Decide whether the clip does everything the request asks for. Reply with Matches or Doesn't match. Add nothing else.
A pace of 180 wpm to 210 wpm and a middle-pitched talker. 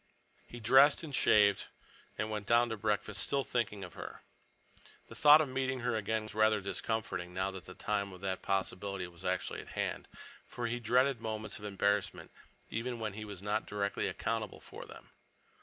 Doesn't match